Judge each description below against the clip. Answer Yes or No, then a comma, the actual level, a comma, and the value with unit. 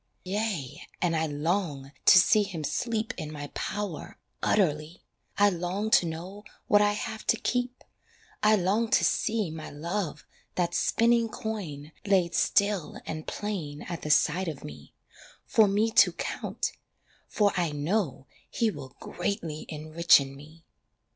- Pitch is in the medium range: Yes, medium, 180 Hz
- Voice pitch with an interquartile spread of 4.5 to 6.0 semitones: Yes, average, 5.2 semitones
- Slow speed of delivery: No, average, 145 wpm